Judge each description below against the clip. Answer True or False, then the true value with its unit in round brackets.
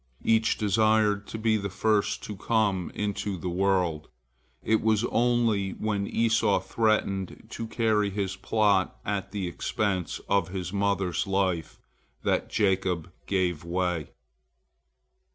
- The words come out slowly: True (125 wpm)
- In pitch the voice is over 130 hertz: False (100 Hz)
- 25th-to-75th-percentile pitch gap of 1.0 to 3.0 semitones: True (2.6 semitones)